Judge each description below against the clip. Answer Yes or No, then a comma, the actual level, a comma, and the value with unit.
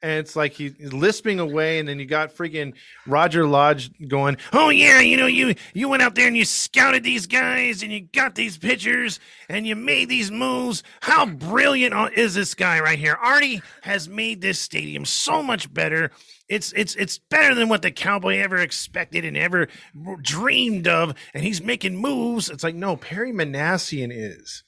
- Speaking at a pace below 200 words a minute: Yes, average, 190 wpm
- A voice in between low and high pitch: No, high, 200 Hz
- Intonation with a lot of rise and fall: Yes, wide, 7.5 semitones